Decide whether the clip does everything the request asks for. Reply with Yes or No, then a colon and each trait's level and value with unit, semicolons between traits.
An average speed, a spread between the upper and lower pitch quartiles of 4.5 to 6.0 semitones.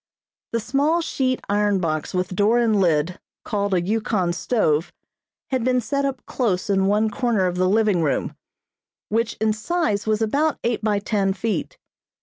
No: average, 165 wpm; average, 4.1 semitones